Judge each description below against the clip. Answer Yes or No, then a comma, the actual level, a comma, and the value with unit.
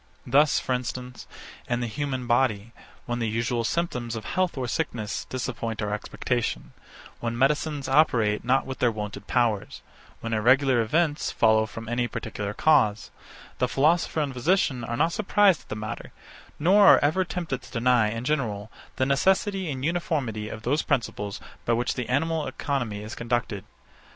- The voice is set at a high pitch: No, low, 125 Hz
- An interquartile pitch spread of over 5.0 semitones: No, average, 4.5 semitones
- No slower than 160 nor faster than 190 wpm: Yes, average, 165 wpm